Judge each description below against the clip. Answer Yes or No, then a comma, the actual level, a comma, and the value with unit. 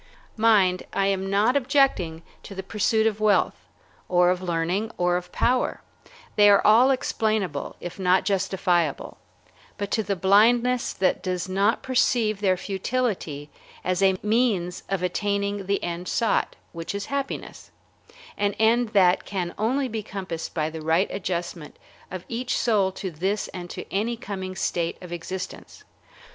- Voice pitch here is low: No, high, 195 Hz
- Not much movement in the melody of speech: No, average, 3.4 semitones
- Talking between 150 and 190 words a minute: Yes, average, 155 wpm